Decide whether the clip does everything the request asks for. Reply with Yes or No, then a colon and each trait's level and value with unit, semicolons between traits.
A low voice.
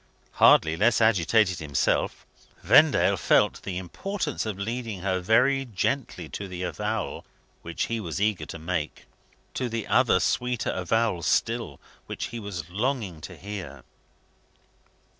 Yes: low, 100 Hz